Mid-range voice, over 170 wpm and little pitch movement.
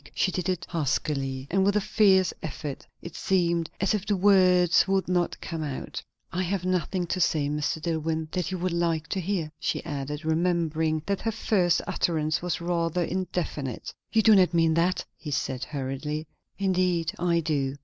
No: medium, 170 Hz; average, 180 wpm; average, 3.0 semitones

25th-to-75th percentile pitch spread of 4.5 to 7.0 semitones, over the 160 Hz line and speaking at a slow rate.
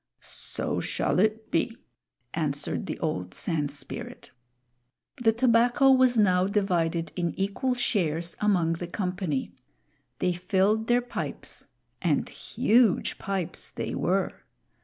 Yes: average, 5.1 semitones; high, 190 Hz; slow, 115 wpm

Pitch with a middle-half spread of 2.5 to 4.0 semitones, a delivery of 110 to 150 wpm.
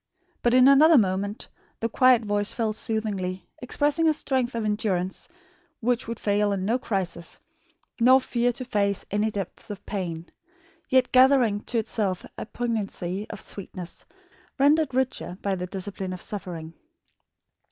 No: average, 4.4 semitones; average, 145 wpm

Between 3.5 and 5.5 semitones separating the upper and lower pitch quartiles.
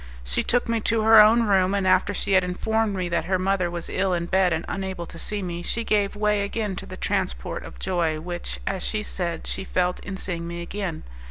No: average, 3.0 semitones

